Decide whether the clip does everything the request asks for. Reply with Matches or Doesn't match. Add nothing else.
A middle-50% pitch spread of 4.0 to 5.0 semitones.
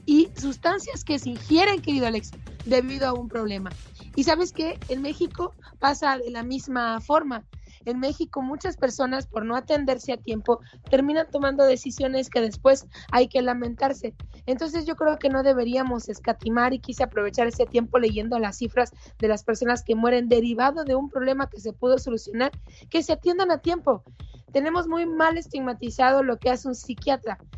Doesn't match